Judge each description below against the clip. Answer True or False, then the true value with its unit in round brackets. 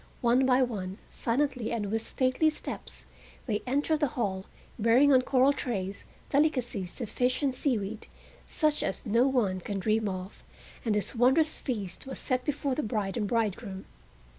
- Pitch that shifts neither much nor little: True (4.4 semitones)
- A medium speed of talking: True (165 wpm)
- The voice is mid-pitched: False (240 Hz)